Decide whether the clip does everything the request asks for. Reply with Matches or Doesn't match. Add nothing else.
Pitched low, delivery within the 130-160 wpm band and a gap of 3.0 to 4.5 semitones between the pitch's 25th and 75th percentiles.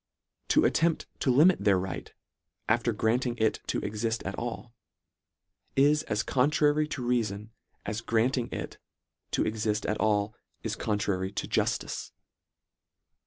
Matches